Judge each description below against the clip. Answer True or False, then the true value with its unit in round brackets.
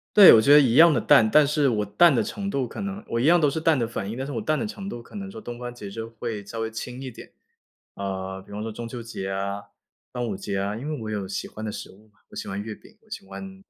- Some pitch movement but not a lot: False (6.2 semitones)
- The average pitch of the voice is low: True (115 Hz)